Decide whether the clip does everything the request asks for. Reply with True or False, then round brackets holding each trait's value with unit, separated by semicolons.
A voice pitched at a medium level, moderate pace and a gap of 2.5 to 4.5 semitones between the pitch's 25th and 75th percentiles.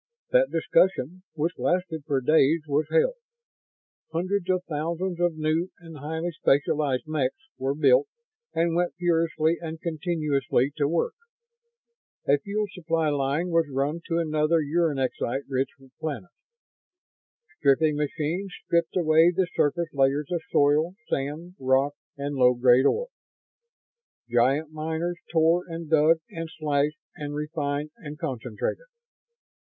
False (155 Hz; 125 wpm; 3.0 semitones)